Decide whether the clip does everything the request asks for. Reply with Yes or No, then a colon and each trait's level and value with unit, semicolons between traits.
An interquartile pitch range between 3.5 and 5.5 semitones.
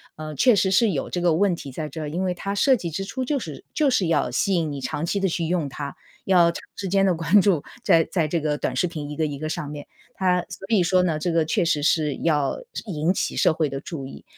Yes: average, 3.8 semitones